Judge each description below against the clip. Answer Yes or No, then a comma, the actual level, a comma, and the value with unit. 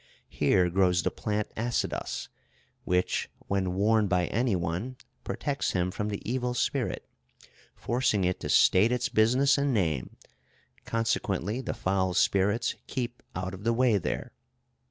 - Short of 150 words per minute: Yes, average, 140 wpm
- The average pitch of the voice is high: No, low, 105 Hz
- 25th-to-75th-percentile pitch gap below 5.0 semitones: Yes, average, 4.6 semitones